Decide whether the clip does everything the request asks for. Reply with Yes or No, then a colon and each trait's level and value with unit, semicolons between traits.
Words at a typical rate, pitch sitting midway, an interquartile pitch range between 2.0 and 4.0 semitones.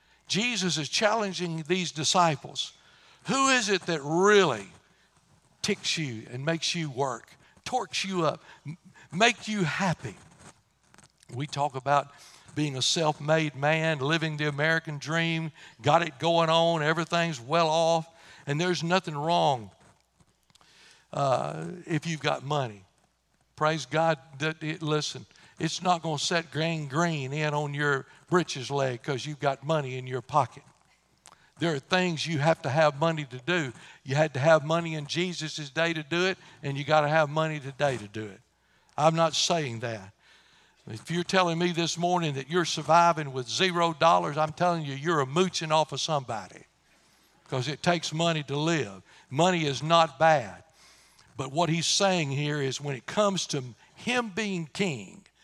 Yes: average, 165 wpm; medium, 160 Hz; average, 3.0 semitones